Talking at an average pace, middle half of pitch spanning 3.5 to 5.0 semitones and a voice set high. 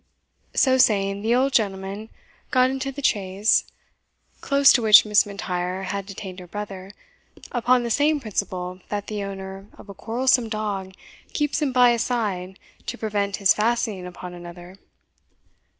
Yes: average, 150 wpm; average, 4.0 semitones; high, 205 Hz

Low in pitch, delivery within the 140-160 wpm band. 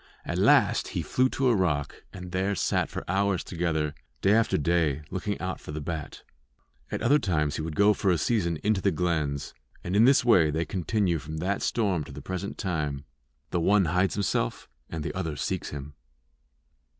No: very low, 85 Hz; average, 195 wpm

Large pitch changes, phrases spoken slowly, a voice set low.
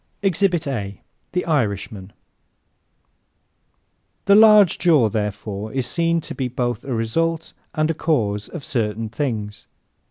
Yes: wide, 7.5 semitones; slow, 130 wpm; low, 125 Hz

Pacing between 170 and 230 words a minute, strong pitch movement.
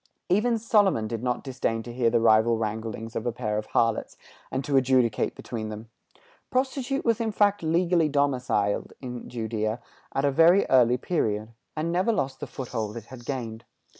Yes: average, 175 wpm; wide, 6.6 semitones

